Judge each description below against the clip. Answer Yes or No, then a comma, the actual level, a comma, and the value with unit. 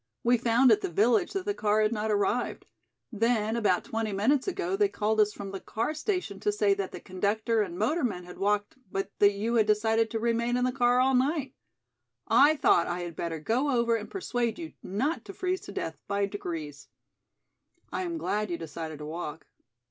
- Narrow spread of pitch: No, average, 3.9 semitones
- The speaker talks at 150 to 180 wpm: No, fast, 205 wpm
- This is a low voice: No, high, 220 Hz